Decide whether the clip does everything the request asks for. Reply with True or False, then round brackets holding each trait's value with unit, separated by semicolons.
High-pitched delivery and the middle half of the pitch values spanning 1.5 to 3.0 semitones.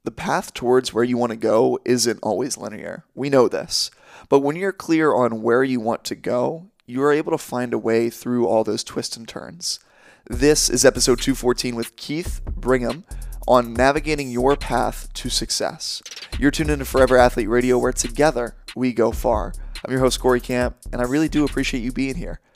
False (125 Hz; 2.4 semitones)